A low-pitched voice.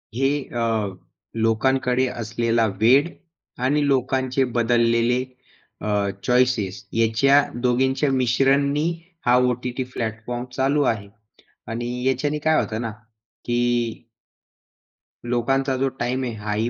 Yes: low, 125 Hz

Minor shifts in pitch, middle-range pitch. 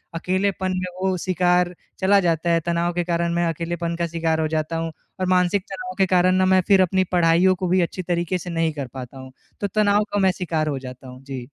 Yes: narrow, 2.3 semitones; medium, 175 Hz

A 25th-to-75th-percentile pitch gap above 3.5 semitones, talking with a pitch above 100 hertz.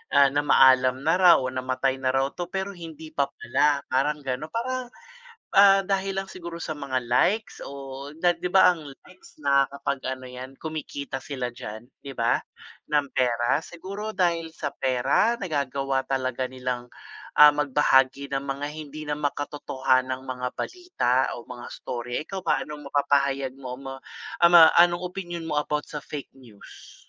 Yes: average, 4.0 semitones; medium, 140 Hz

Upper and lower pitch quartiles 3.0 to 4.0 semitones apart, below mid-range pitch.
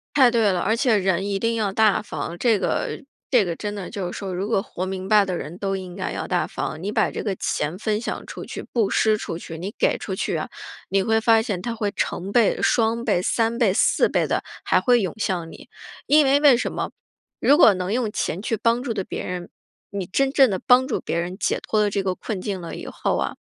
No: average, 3.7 semitones; high, 205 Hz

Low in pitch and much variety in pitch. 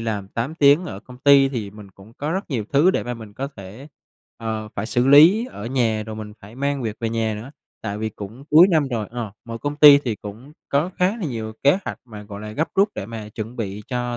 No: low, 115 Hz; average, 4.7 semitones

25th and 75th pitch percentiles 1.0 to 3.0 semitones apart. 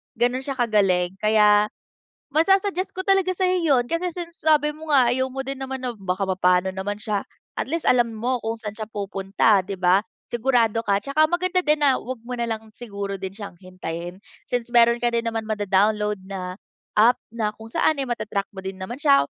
No: average, 5.2 semitones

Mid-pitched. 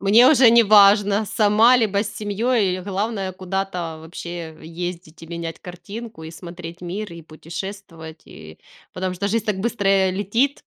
No: high, 195 Hz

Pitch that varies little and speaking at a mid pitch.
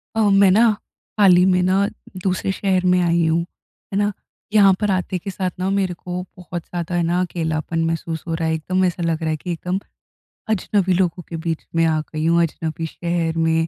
Yes: narrow, 2.2 semitones; medium, 175 Hz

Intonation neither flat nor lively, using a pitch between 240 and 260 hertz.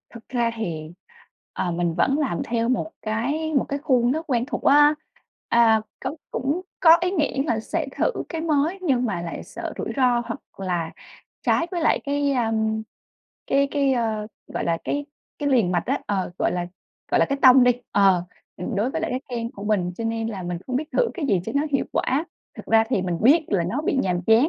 No: wide, 5.8 semitones; high, 245 Hz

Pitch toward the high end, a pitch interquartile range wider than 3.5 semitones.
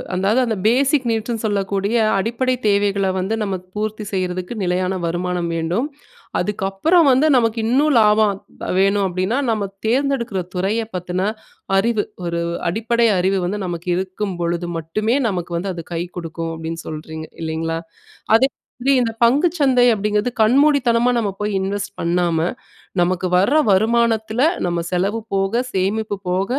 Yes: high, 200 Hz; average, 4.3 semitones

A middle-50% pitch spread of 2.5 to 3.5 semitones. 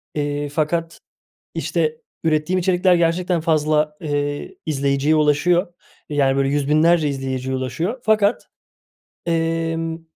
Yes: average, 2.8 semitones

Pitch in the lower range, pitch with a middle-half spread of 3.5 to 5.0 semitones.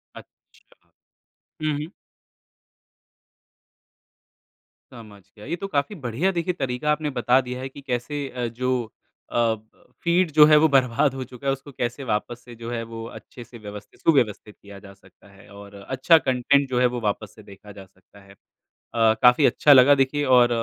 Yes: low, 125 Hz; average, 4.1 semitones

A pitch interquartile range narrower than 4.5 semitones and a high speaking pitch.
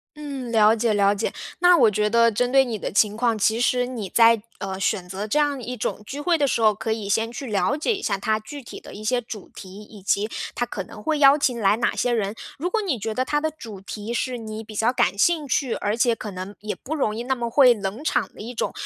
Yes: average, 3.6 semitones; high, 230 Hz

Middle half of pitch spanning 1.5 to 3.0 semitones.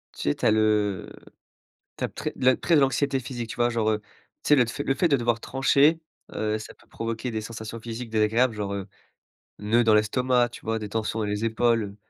Yes: average, 2.7 semitones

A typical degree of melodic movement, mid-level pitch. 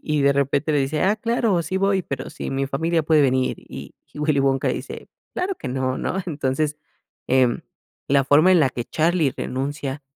Yes: average, 3.9 semitones; medium, 145 Hz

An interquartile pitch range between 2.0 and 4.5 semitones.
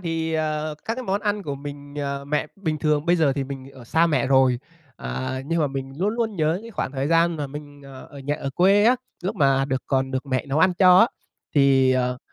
Yes: average, 3.8 semitones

